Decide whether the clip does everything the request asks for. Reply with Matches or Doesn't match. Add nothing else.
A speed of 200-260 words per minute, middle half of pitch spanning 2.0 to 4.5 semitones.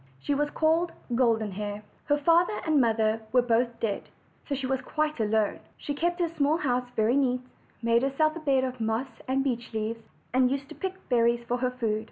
Matches